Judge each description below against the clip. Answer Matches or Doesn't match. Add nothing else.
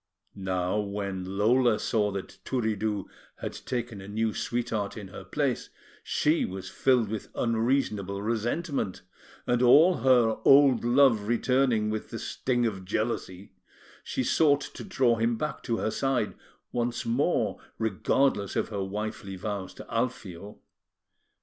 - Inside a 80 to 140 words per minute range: Matches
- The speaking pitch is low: Matches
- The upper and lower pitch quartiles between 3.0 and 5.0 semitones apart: Matches